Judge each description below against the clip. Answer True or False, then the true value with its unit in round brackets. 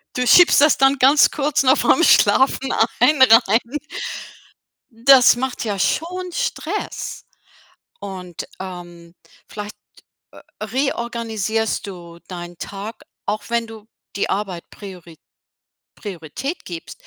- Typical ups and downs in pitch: False (5.8 semitones)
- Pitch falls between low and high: False (225 Hz)